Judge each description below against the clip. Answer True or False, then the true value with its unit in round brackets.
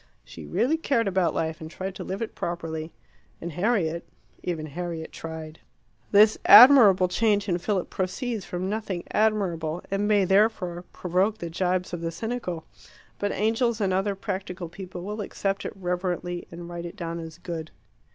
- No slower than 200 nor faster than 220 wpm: False (165 wpm)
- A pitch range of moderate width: True (3.3 semitones)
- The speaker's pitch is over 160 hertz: True (185 Hz)